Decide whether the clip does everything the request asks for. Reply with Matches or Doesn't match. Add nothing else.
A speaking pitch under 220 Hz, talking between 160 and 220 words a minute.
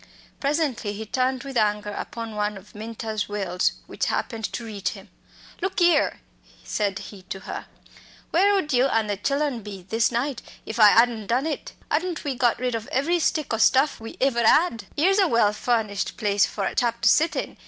Doesn't match